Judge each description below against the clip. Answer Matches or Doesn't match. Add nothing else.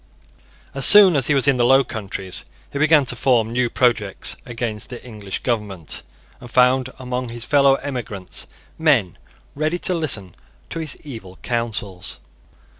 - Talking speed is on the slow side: Doesn't match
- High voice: Doesn't match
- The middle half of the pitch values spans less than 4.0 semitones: Doesn't match